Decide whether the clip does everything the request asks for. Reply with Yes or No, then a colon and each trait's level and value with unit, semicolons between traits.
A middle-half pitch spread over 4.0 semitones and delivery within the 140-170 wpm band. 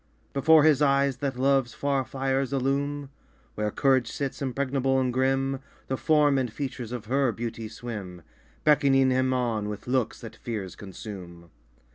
No: average, 3.0 semitones; average, 150 wpm